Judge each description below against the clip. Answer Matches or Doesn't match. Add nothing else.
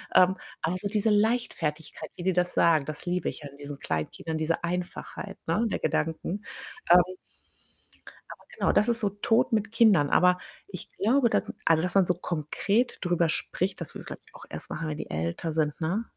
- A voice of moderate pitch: Matches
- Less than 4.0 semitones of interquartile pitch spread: Doesn't match